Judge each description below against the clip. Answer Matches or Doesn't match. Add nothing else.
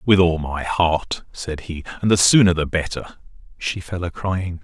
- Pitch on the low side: Matches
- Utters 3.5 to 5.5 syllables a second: Matches